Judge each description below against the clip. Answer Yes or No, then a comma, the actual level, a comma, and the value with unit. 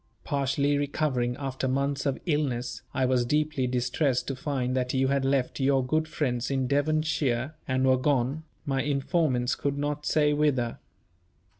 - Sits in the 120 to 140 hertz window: Yes, low, 135 Hz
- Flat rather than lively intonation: Yes, narrow, 2.3 semitones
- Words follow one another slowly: No, average, 155 wpm